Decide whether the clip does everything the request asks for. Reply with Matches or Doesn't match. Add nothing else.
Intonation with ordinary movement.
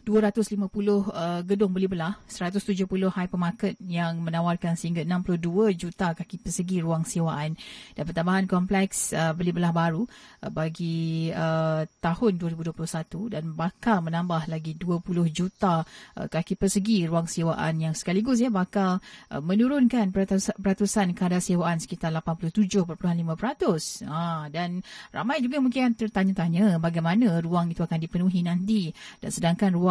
Matches